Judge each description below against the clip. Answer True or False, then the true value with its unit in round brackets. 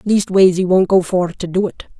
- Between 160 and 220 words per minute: False (240 wpm)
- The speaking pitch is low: False (185 Hz)